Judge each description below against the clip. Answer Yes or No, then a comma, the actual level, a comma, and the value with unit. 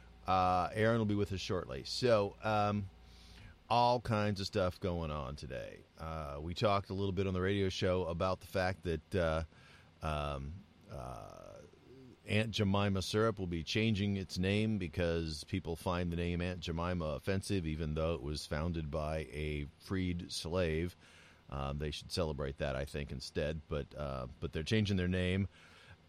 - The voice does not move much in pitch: No, average, 3.7 semitones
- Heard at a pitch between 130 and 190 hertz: No, very low, 85 Hz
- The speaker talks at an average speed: Yes, average, 170 wpm